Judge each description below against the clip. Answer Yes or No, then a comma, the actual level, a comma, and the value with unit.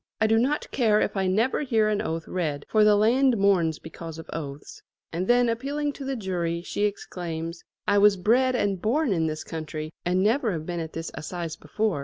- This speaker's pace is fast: Yes, fast, 210 wpm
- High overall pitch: Yes, high, 195 Hz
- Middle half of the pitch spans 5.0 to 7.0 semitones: Yes, wide, 5.5 semitones